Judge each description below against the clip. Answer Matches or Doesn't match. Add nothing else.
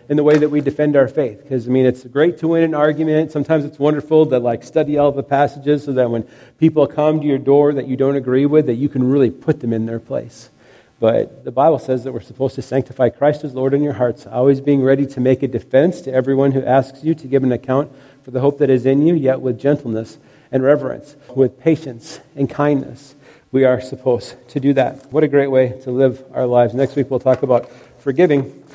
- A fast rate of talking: Matches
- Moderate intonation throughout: Doesn't match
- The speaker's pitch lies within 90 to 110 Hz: Doesn't match